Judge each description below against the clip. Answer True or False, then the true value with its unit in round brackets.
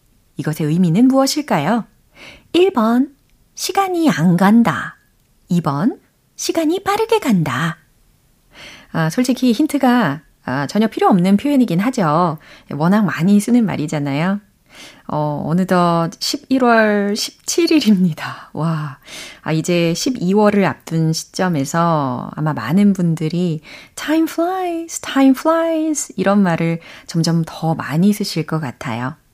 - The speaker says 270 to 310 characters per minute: False (245 characters per minute)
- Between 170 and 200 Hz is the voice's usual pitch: True (190 Hz)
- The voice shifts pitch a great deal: True (8.4 semitones)